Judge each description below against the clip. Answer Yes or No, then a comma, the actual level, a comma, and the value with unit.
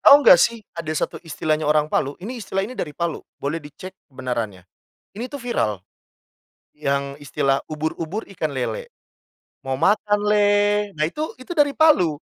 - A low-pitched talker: No, medium, 170 Hz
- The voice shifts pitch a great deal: Yes, wide, 6.4 semitones